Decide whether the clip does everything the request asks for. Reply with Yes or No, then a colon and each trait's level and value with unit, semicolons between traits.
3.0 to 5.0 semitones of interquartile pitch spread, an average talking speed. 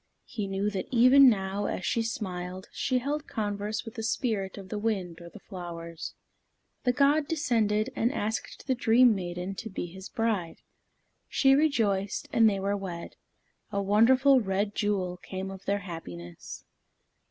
Yes: average, 3.6 semitones; average, 160 wpm